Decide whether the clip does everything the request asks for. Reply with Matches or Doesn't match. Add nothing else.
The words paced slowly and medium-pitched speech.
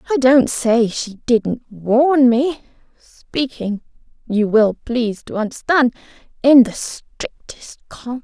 Doesn't match